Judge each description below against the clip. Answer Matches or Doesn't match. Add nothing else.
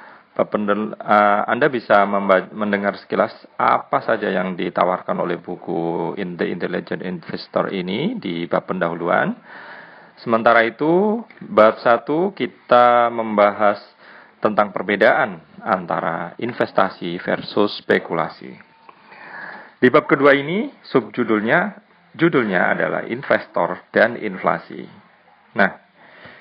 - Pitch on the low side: Matches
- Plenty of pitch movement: Matches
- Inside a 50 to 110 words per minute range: Matches